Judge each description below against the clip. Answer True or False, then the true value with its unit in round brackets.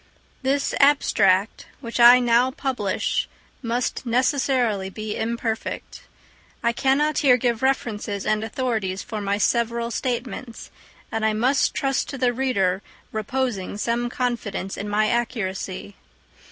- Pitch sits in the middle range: False (235 Hz)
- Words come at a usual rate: False (125 wpm)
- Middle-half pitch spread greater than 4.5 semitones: False (3.4 semitones)